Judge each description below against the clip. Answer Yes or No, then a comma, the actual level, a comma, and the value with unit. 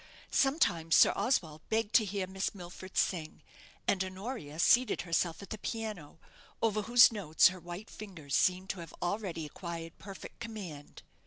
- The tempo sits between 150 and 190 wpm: Yes, average, 155 wpm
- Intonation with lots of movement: No, average, 4.4 semitones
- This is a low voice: No, medium, 185 Hz